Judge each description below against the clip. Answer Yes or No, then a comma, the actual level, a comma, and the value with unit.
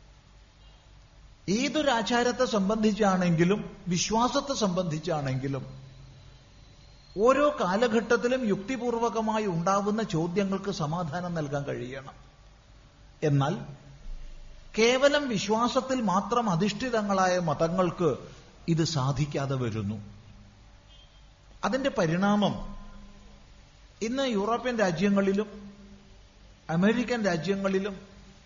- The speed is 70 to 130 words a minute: No, slow, 60 wpm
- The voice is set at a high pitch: Yes, high, 195 Hz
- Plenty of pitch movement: Yes, wide, 7.3 semitones